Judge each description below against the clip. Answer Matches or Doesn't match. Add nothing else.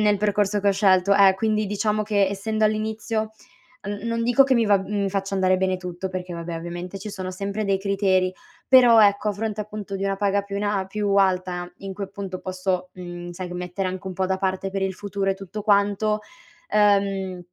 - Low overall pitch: Doesn't match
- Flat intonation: Matches